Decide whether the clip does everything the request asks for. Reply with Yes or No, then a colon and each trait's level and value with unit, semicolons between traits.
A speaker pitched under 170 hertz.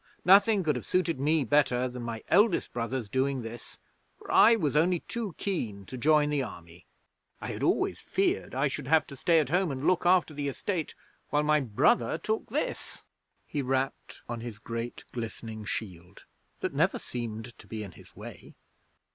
Yes: low, 135 Hz